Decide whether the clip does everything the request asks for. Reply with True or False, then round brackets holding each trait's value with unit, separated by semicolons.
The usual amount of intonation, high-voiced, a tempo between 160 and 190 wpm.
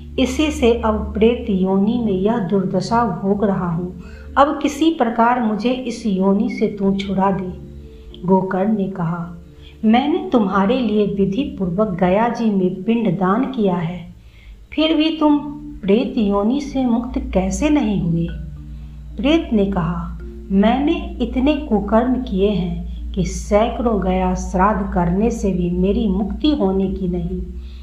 False (4.4 semitones; 205 Hz; 140 wpm)